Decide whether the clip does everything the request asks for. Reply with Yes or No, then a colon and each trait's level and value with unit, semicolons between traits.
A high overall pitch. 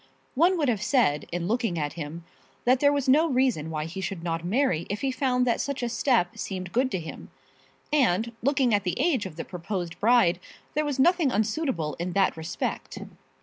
Yes: high, 220 Hz